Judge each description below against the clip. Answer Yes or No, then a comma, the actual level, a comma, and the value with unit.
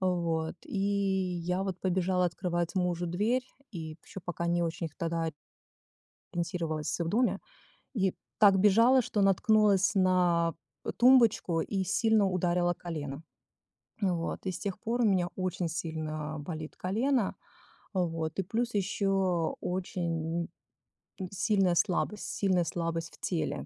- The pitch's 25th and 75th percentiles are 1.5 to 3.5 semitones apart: Yes, average, 2.8 semitones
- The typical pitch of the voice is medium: Yes, medium, 180 Hz